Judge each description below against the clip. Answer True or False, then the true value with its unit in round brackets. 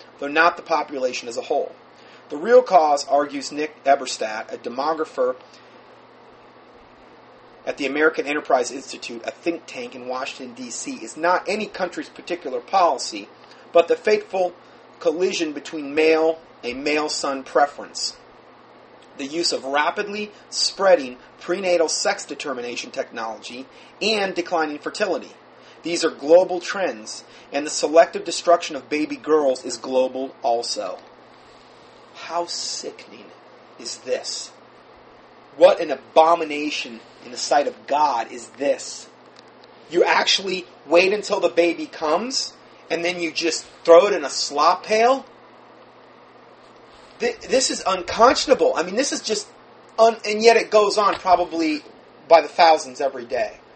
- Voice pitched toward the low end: False (170 Hz)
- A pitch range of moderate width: False (6.1 semitones)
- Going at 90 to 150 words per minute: True (135 wpm)